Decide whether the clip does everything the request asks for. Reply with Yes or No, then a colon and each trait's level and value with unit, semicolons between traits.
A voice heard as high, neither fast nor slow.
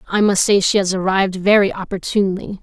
Yes: high, 195 Hz; average, 185 wpm